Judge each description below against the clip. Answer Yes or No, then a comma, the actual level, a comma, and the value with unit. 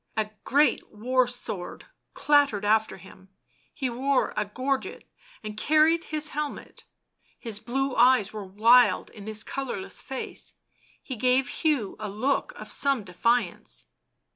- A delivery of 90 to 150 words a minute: Yes, slow, 135 wpm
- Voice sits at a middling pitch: No, high, 240 Hz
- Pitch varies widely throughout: No, average, 4.4 semitones